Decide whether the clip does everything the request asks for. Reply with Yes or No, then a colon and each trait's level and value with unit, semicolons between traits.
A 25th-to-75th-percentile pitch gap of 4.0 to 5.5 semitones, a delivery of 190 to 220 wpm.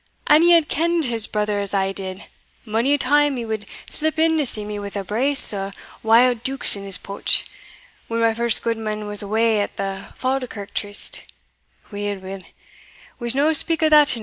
Yes: average, 5.2 semitones; average, 195 wpm